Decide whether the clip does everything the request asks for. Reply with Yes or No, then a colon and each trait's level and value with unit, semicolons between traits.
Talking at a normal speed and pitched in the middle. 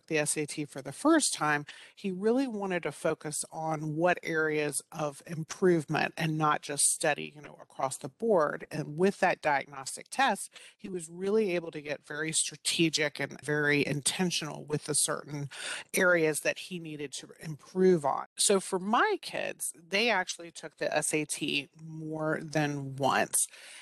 Yes: average, 160 wpm; medium, 160 Hz